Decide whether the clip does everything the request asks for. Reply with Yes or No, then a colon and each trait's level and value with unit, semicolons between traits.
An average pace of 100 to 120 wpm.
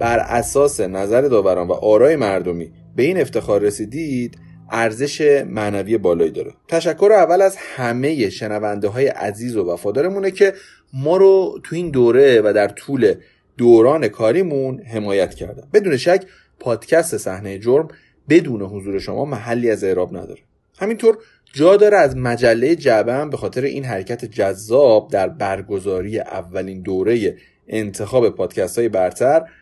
No: average, 140 wpm